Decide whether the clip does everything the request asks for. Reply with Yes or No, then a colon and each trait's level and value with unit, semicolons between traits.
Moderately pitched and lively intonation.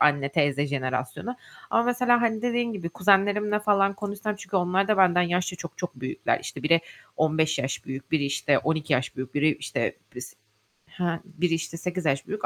Yes: medium, 175 Hz; wide, 5.7 semitones